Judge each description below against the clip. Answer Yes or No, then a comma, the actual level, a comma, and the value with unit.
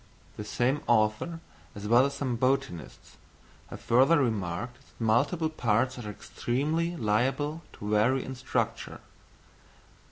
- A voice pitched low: Yes, low, 125 Hz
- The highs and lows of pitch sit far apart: No, average, 4.4 semitones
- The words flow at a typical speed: No, slow, 125 wpm